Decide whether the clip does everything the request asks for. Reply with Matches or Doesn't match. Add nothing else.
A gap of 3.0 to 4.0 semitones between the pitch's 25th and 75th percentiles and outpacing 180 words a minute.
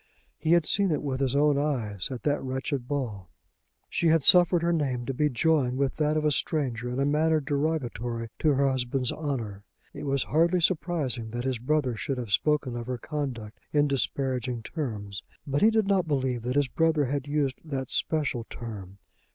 Matches